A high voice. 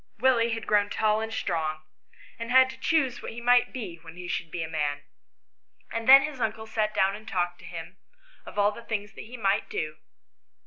Yes: high, 215 Hz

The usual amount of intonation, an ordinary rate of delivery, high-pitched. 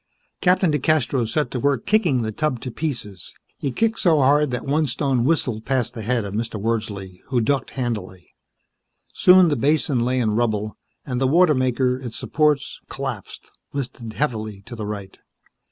No: average, 4.6 semitones; average, 170 wpm; low, 125 Hz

